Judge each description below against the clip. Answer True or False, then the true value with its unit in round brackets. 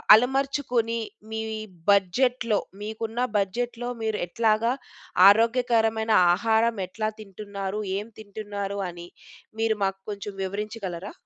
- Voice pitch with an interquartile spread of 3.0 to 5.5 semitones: False (2.4 semitones)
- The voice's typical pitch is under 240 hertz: True (220 Hz)